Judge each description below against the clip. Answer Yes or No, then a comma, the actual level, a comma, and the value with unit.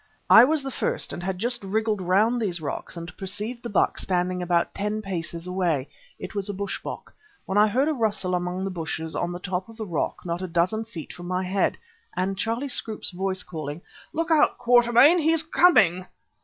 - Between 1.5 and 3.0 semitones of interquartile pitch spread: No, average, 4.2 semitones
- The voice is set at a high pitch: Yes, high, 195 Hz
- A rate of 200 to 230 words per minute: Yes, fast, 205 wpm